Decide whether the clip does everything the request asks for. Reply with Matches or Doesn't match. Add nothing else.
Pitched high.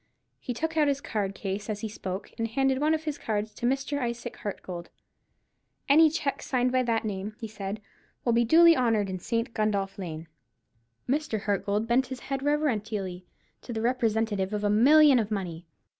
Matches